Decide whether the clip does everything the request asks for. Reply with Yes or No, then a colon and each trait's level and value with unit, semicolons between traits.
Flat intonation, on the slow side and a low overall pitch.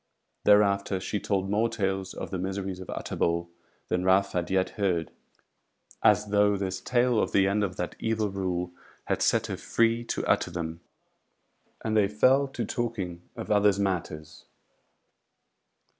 No: narrow, 2.3 semitones; average, 155 wpm; low, 100 Hz